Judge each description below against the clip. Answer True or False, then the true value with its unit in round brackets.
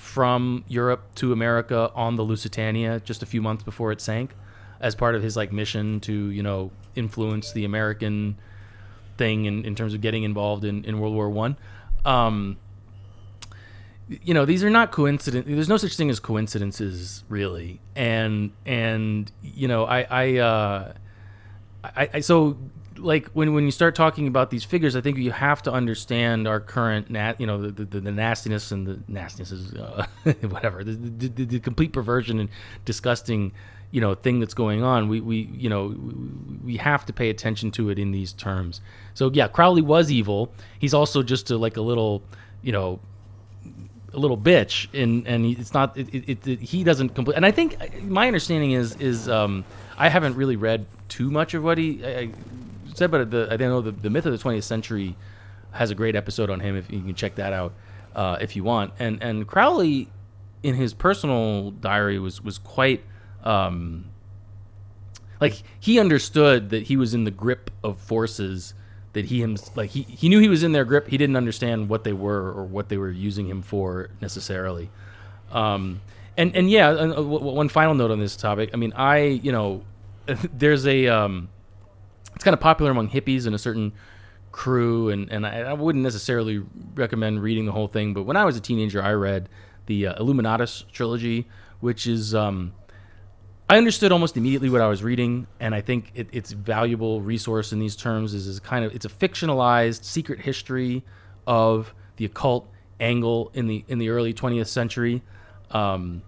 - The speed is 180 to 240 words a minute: True (190 wpm)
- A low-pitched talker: True (110 Hz)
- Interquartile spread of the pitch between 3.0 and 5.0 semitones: True (3.8 semitones)